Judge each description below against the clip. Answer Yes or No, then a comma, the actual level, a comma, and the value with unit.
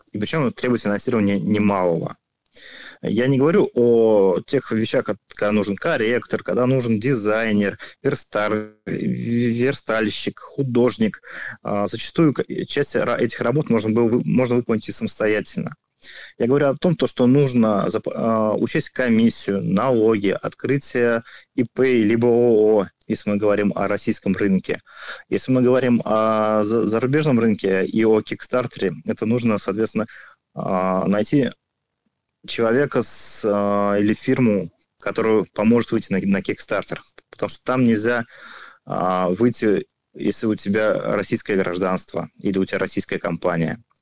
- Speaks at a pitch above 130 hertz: No, low, 110 Hz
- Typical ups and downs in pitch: Yes, average, 3.3 semitones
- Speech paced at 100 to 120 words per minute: Yes, slow, 110 wpm